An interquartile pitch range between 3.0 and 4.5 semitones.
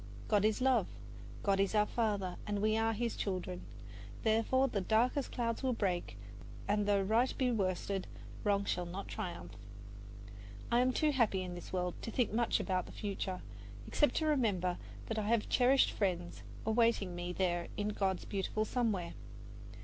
Yes: average, 3.9 semitones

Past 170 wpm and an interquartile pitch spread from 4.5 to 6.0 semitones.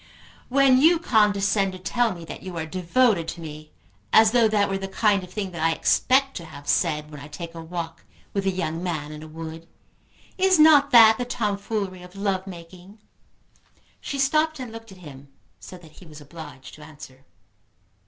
Yes: average, 195 wpm; wide, 5.4 semitones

